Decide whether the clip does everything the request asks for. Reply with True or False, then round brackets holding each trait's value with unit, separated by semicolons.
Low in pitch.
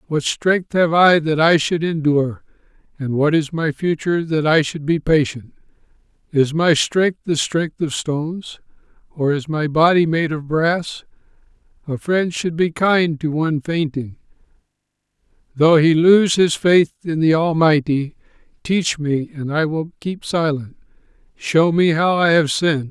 False (160 Hz)